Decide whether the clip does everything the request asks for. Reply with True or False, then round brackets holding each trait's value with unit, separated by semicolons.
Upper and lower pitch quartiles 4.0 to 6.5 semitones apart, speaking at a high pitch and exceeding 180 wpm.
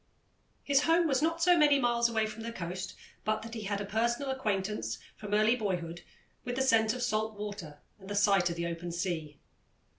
True (4.4 semitones; 215 Hz; 205 wpm)